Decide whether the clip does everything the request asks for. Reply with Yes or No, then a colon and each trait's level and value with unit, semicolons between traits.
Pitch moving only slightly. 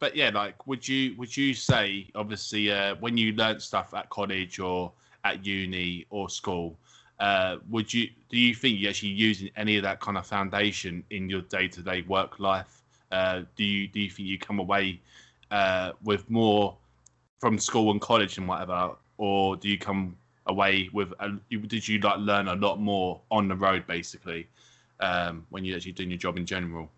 Yes: narrow, 2.3 semitones